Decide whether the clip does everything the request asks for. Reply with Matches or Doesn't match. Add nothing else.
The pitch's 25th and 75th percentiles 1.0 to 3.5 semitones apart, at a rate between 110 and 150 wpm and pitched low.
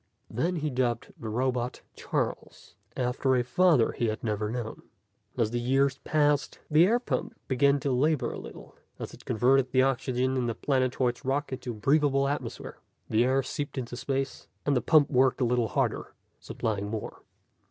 Doesn't match